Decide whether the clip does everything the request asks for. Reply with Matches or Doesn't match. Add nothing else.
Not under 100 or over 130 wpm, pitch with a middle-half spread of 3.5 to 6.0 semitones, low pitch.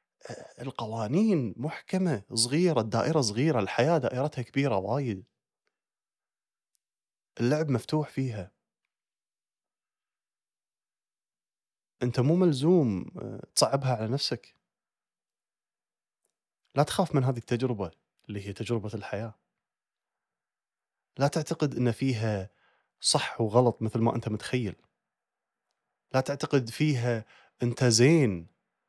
Doesn't match